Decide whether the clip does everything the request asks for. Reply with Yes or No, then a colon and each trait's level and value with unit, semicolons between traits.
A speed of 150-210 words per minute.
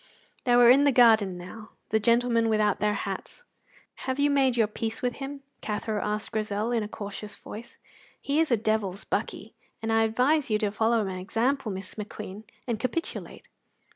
Yes: average, 180 wpm